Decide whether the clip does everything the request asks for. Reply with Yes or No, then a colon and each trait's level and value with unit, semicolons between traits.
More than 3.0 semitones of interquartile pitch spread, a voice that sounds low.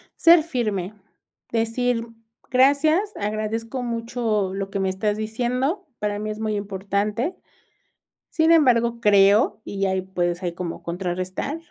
No: average, 4.1 semitones; high, 215 Hz